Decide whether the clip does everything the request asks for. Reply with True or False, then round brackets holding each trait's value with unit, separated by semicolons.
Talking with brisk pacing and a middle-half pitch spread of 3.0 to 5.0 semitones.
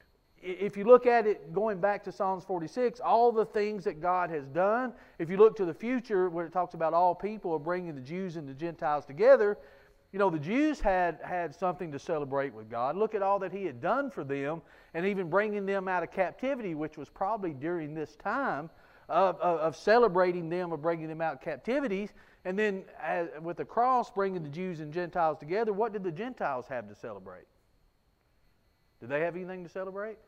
True (210 wpm; 3.9 semitones)